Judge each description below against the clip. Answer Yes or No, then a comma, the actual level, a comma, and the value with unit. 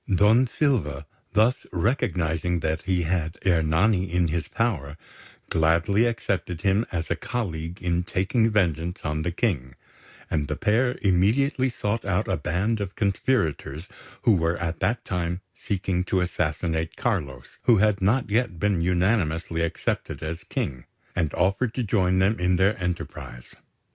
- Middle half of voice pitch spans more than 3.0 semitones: Yes, average, 4.3 semitones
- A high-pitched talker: No, very low, 90 Hz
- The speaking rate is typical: Yes, average, 150 wpm